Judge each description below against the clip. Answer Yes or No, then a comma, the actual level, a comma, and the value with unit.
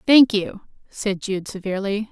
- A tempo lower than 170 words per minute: Yes, average, 140 wpm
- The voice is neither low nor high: No, high, 205 Hz